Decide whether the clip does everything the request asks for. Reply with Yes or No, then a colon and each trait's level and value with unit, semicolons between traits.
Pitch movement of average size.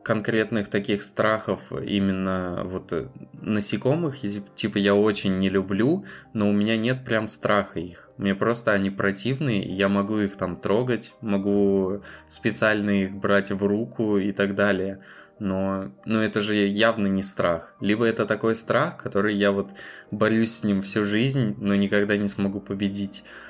No: narrow, 1.7 semitones